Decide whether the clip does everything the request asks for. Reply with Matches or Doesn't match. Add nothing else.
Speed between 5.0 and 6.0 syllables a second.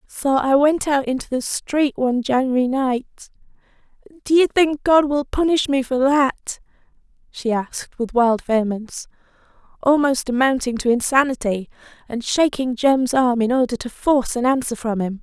Doesn't match